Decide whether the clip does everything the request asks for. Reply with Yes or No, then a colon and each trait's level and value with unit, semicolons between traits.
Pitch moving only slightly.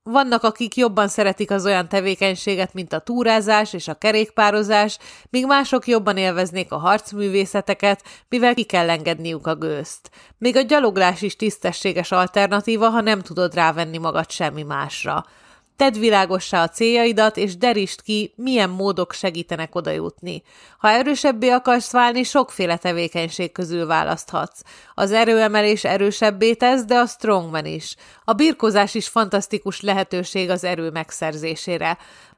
No: average, 4.0 semitones